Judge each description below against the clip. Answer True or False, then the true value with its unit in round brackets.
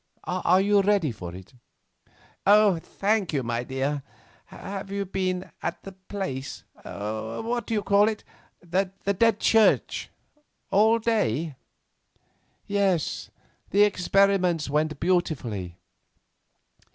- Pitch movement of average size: False (5.7 semitones)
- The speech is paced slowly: True (105 wpm)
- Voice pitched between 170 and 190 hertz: True (185 Hz)